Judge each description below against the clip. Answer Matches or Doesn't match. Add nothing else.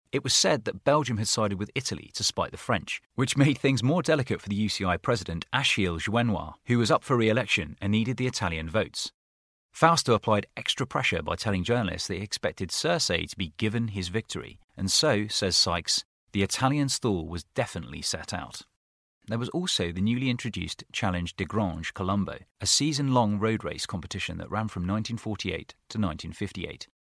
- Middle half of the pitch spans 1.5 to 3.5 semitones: Doesn't match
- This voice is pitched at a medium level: Doesn't match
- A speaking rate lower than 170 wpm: Doesn't match